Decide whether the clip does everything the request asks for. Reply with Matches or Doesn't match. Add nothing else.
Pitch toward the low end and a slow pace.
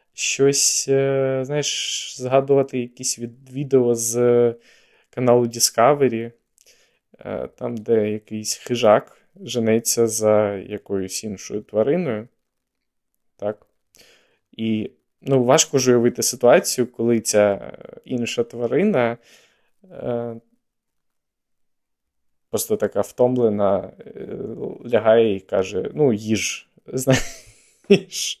Matches